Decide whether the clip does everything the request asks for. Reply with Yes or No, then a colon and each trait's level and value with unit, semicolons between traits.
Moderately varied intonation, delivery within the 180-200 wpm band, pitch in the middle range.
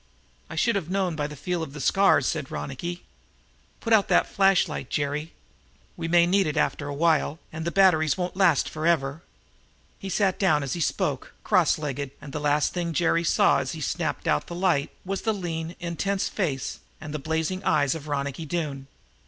Yes: average, 3.5 semitones; average, 195 wpm; medium, 160 Hz